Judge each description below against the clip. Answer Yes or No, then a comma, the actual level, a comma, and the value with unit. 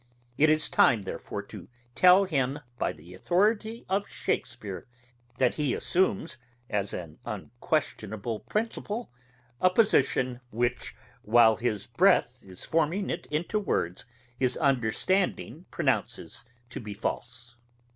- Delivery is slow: Yes, slow, 120 wpm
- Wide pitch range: Yes, wide, 8.4 semitones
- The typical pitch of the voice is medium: No, low, 125 Hz